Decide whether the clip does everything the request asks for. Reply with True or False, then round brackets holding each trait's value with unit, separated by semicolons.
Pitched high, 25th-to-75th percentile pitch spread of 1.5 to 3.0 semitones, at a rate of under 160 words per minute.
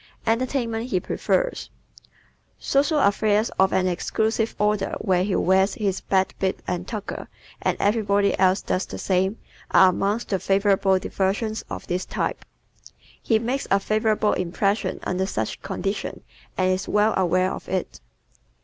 True (200 Hz; 2.5 semitones; 150 wpm)